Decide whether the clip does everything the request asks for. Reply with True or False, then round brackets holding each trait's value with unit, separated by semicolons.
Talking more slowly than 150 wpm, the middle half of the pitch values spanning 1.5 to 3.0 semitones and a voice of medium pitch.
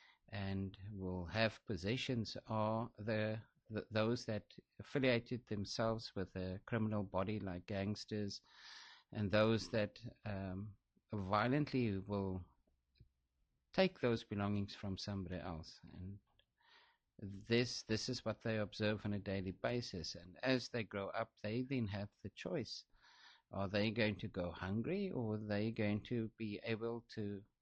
False (140 wpm; 2.7 semitones; 105 Hz)